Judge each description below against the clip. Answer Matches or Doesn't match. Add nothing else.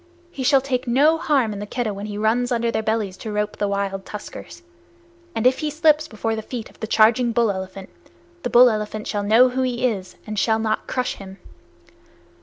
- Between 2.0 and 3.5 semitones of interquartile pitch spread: Matches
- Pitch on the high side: Matches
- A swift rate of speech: Matches